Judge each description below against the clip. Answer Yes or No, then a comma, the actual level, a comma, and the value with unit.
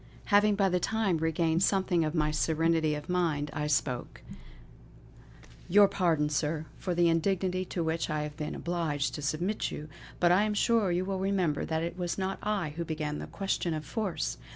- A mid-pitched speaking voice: Yes, medium, 170 Hz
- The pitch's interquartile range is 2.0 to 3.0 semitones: No, average, 3.8 semitones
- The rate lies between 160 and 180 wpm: No, average, 190 wpm